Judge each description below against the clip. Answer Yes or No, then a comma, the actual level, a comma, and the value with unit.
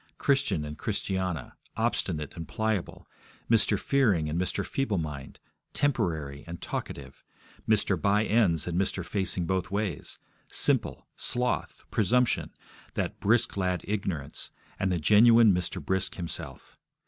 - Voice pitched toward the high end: No, very low, 95 Hz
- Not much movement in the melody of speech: No, average, 4.7 semitones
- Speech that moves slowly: Yes, slow, 125 wpm